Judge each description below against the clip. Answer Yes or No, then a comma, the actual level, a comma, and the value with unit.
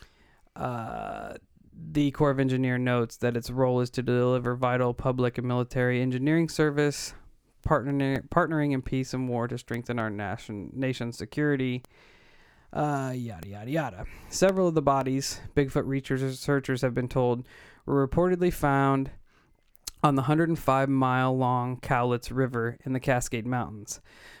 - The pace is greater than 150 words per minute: No, average, 140 wpm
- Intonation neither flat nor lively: No, narrow, 2.3 semitones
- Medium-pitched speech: No, low, 130 Hz